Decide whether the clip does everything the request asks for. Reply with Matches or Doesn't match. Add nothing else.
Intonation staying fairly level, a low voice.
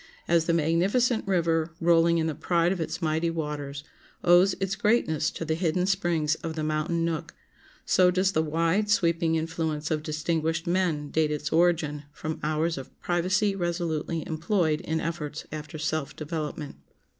Doesn't match